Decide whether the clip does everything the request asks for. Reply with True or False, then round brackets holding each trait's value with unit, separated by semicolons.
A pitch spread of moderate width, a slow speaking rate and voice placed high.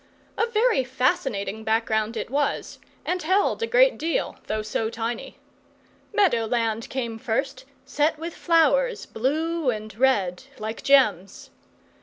False (7.0 semitones; 130 wpm; 260 Hz)